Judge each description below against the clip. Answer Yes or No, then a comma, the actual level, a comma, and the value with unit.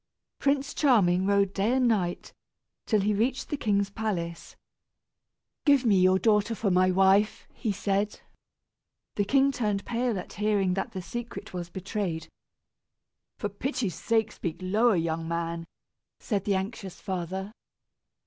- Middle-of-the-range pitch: No, high, 200 Hz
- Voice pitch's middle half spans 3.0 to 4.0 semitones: Yes, average, 3.3 semitones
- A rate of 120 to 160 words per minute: Yes, average, 140 wpm